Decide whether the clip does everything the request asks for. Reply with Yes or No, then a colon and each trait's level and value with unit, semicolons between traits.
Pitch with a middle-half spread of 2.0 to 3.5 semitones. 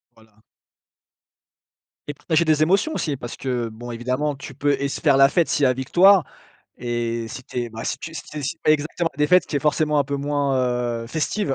No: average, 3.9 semitones